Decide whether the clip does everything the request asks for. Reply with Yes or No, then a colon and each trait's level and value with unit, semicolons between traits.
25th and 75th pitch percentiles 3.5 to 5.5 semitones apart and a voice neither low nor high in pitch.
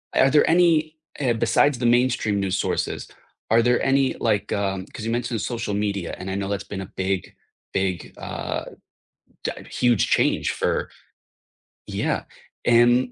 No: average, 4.1 semitones; low, 115 Hz